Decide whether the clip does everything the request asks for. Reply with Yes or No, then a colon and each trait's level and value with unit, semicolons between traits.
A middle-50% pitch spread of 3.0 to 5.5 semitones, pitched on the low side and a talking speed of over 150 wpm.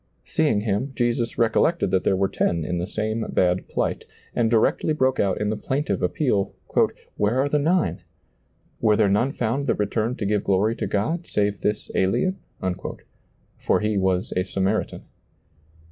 Yes: average, 4.8 semitones; low, 110 Hz; average, 175 wpm